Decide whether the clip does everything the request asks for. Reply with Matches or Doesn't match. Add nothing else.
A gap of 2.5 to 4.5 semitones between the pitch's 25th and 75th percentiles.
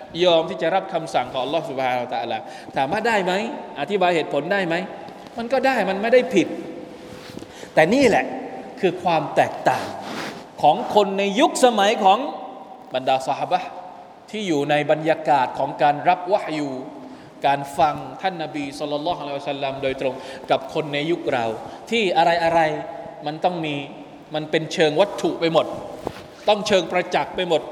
Doesn't match